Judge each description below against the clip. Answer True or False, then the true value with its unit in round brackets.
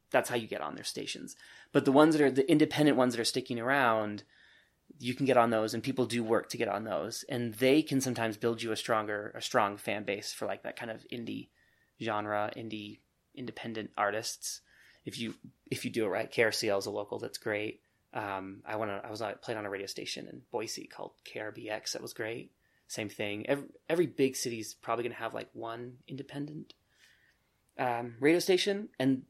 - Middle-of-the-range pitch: False (120 Hz)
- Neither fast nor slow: False (215 wpm)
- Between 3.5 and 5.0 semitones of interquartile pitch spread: True (3.8 semitones)